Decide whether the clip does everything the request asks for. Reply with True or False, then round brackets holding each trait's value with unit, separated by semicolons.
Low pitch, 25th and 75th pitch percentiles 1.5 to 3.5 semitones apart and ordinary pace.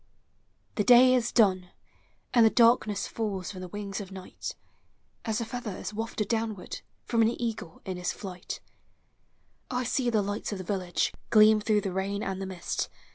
False (210 Hz; 3.1 semitones; 185 wpm)